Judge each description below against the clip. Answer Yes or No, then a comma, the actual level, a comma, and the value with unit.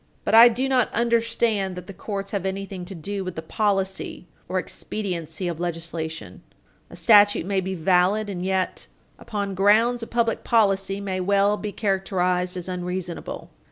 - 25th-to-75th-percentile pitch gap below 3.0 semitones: Yes, narrow, 2.5 semitones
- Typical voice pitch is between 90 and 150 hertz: No, high, 195 Hz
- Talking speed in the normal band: Yes, average, 160 wpm